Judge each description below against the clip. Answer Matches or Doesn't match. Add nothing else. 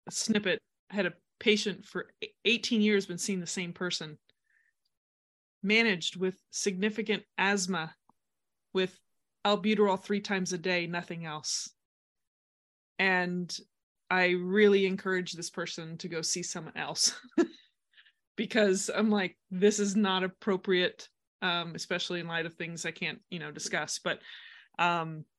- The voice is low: Doesn't match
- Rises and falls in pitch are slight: Doesn't match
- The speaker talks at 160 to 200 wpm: Doesn't match